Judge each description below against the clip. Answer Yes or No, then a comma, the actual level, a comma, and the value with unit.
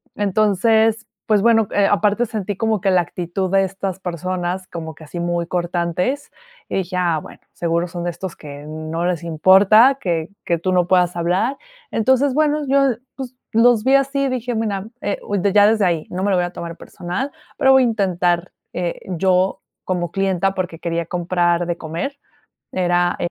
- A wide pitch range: No, average, 4.1 semitones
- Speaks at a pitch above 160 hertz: Yes, medium, 185 Hz